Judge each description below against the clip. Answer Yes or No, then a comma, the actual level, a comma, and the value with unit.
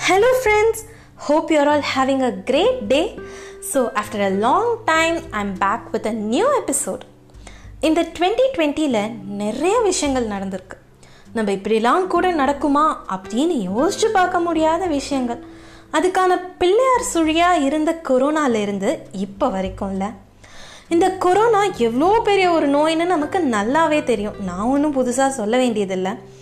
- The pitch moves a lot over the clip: Yes, wide, 8.3 semitones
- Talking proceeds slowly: No, average, 125 wpm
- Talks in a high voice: Yes, very high, 295 Hz